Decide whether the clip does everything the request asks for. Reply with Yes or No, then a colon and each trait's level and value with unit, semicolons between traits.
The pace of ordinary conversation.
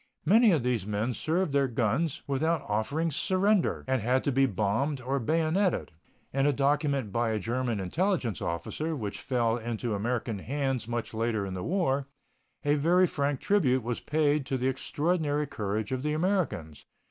Yes: average, 170 wpm